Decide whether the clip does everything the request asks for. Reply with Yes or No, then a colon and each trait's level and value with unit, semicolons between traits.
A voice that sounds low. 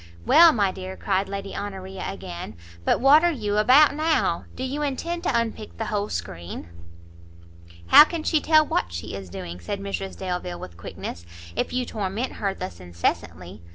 No: high, 200 Hz